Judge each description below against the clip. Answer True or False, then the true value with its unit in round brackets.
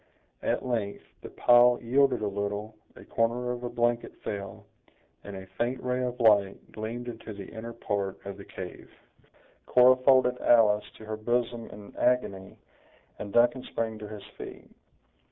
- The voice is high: False (115 Hz)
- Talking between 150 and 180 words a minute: True (160 wpm)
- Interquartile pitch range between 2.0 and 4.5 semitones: True (3.2 semitones)